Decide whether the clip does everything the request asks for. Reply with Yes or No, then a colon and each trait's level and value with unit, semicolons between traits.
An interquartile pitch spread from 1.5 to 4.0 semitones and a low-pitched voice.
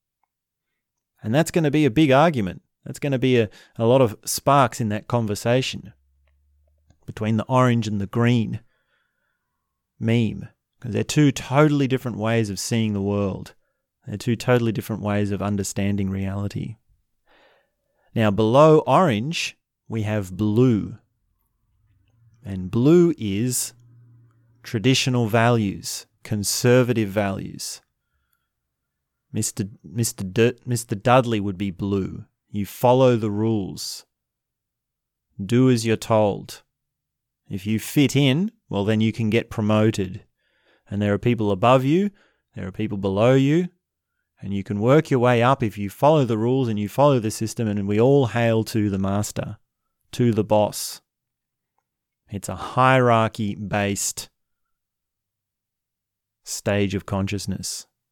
Yes: average, 3.5 semitones; low, 110 Hz